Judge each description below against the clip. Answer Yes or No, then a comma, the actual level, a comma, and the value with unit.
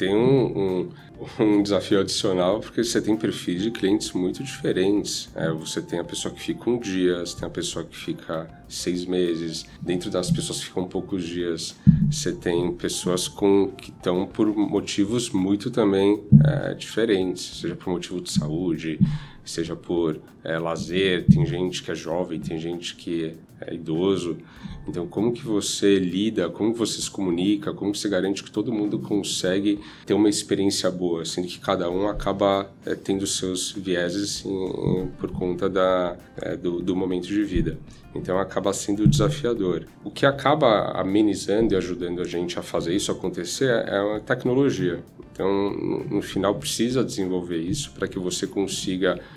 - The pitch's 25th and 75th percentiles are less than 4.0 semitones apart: Yes, narrow, 2.6 semitones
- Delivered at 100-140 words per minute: No, average, 170 wpm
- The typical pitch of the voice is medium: No, very low, 95 Hz